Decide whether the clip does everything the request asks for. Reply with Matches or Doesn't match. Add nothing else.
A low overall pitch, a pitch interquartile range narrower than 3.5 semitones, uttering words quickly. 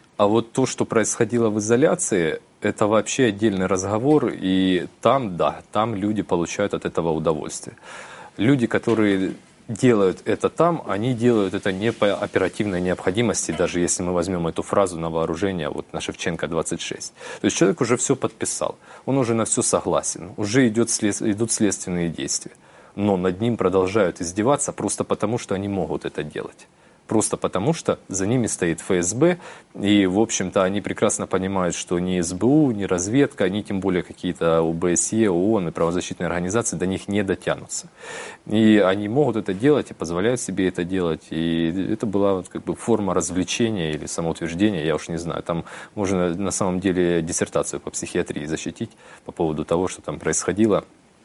Doesn't match